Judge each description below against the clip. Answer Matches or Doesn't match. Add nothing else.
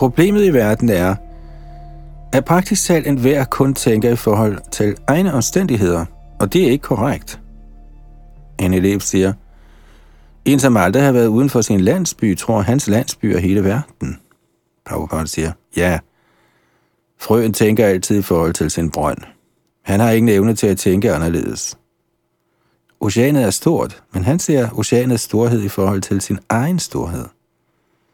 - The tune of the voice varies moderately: Doesn't match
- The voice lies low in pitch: Matches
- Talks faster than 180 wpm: Doesn't match